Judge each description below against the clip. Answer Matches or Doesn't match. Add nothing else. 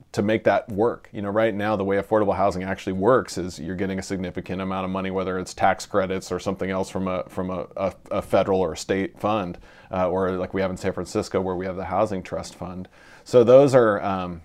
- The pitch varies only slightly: Matches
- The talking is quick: Matches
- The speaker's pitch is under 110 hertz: Matches